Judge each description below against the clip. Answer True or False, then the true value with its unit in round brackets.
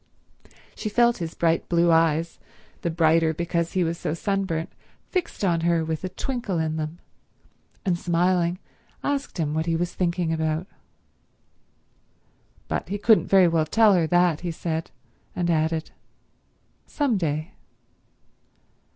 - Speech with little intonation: True (2.3 semitones)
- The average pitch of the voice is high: False (170 Hz)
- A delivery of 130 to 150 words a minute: True (140 wpm)